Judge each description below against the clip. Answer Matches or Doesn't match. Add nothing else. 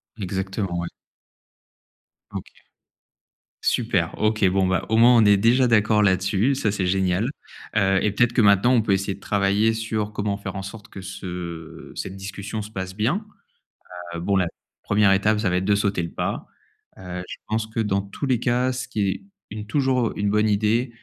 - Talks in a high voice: Doesn't match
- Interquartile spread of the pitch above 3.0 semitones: Doesn't match